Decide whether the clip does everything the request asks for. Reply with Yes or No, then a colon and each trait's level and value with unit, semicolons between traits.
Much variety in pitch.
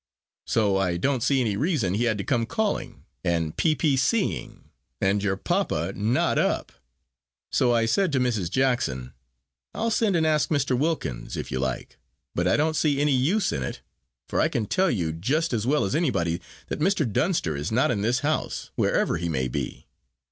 Yes: wide, 8.4 semitones